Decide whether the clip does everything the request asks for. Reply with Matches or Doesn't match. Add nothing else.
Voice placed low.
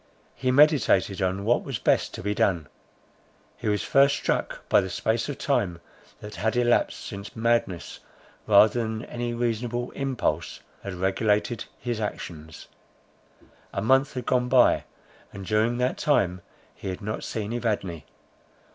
Matches